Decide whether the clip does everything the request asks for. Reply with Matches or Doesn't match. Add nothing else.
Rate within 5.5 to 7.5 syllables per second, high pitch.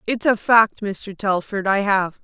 Doesn't match